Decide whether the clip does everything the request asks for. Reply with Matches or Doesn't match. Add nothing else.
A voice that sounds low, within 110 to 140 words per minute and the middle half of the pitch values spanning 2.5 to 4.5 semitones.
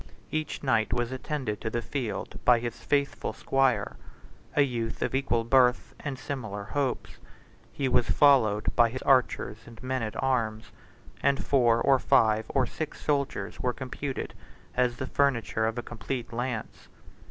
Doesn't match